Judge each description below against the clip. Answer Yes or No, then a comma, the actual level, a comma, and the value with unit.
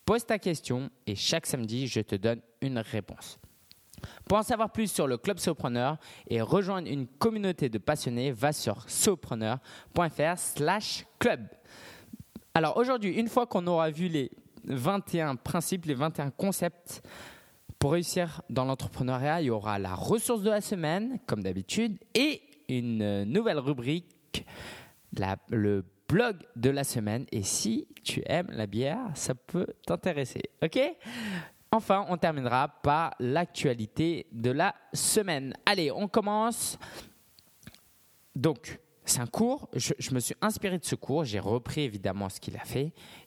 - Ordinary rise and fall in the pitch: No, wide, 8.3 semitones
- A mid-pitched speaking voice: Yes, medium, 150 Hz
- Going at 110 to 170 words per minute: Yes, slow, 145 wpm